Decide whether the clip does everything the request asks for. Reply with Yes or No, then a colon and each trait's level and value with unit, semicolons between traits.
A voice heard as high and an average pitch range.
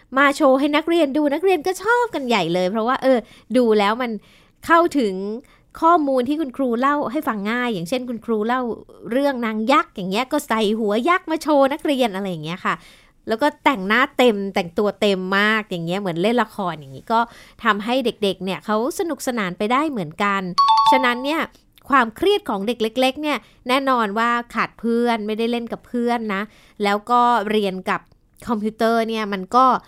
Yes: high, 235 Hz; average, 4.6 semitones